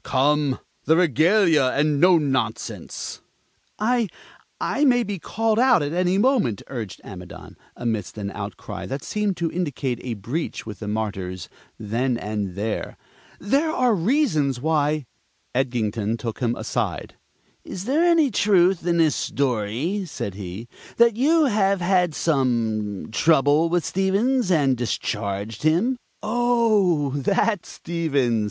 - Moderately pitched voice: Yes, medium, 155 Hz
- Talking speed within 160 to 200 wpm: No, slow, 135 wpm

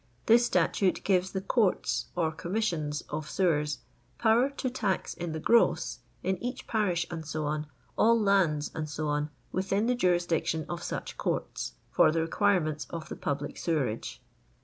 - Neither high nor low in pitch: Yes, medium, 175 Hz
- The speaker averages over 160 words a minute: No, average, 150 wpm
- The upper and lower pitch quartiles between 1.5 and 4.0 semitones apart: No, average, 4.7 semitones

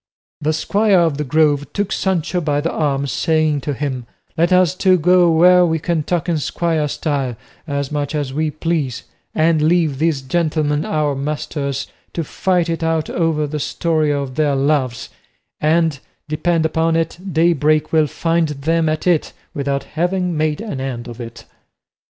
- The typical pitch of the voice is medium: Yes, medium, 155 Hz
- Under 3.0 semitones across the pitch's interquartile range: Yes, narrow, 2.6 semitones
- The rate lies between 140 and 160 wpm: No, average, 170 wpm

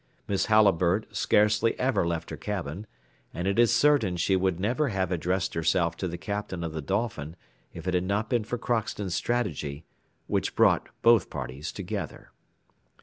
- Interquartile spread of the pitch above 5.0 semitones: No, average, 4.2 semitones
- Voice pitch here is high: No, very low, 95 Hz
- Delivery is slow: No, average, 165 wpm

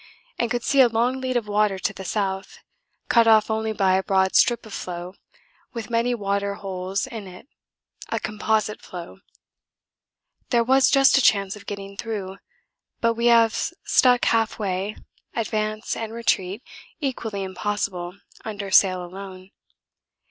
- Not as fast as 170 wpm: Yes, average, 150 wpm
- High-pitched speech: Yes, high, 210 Hz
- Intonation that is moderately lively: Yes, average, 3.2 semitones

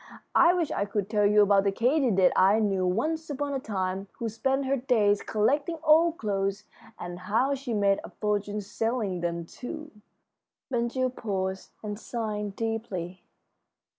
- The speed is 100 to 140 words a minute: No, average, 165 wpm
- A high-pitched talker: Yes, high, 210 Hz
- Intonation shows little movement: No, average, 4.6 semitones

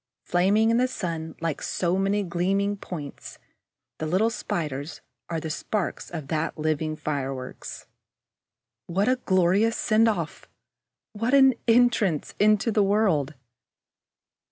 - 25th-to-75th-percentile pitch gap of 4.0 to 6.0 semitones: Yes, average, 5.3 semitones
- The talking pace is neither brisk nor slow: No, slow, 125 wpm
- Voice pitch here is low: No, medium, 185 Hz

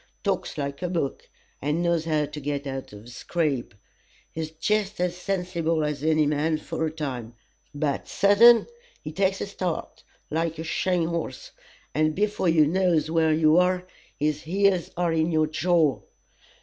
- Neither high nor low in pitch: Yes, medium, 160 Hz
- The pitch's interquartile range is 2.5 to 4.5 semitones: Yes, average, 2.9 semitones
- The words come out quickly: No, average, 165 wpm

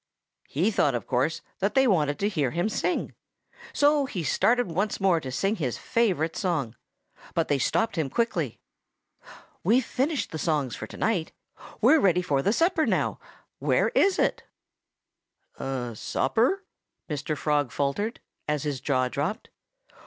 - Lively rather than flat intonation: Yes, wide, 7.9 semitones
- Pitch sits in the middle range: Yes, medium, 170 Hz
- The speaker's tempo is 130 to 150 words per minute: No, average, 160 wpm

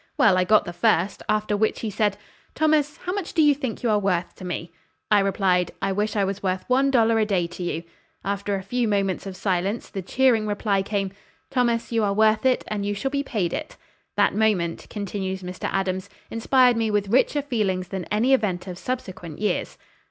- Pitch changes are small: No, average, 3.5 semitones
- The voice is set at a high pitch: Yes, high, 205 Hz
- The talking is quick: Yes, fast, 210 wpm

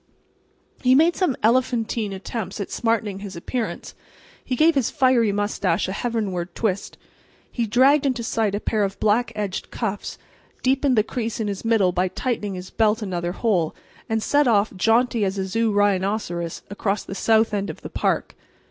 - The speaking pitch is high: Yes, high, 215 Hz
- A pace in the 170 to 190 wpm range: Yes, average, 175 wpm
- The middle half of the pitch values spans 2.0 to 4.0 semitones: Yes, average, 3.4 semitones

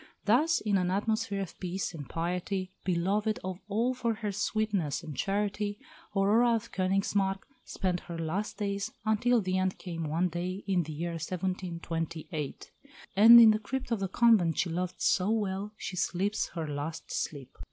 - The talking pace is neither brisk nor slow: Yes, average, 165 wpm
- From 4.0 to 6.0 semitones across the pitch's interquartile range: No, average, 3.5 semitones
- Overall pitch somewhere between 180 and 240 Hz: Yes, high, 190 Hz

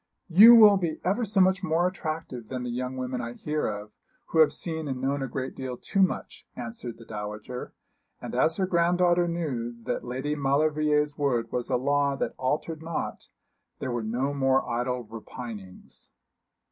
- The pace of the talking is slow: No, average, 175 wpm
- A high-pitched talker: No, medium, 140 Hz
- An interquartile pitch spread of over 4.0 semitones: Yes, average, 4.9 semitones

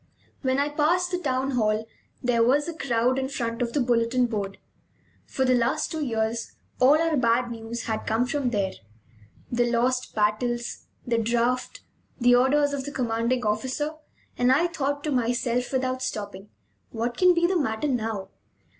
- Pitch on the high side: Yes, high, 245 Hz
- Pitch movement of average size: Yes, average, 3.2 semitones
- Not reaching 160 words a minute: No, average, 170 wpm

